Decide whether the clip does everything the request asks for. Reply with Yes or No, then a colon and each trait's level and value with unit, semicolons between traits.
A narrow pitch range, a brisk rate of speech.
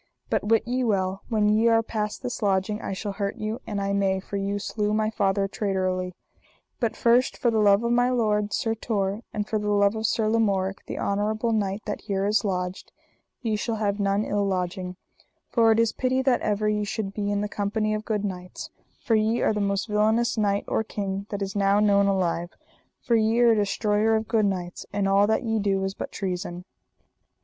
Yes: narrow, 1.9 semitones; fast, 215 wpm